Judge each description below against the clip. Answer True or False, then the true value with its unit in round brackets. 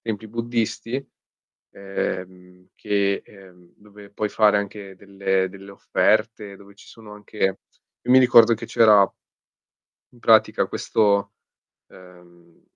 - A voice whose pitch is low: True (100 Hz)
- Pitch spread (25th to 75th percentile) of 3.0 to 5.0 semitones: False (2.4 semitones)